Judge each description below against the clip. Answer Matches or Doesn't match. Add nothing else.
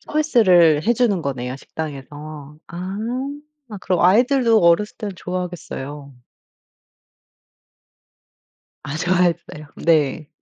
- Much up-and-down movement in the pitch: Doesn't match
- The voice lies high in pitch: Doesn't match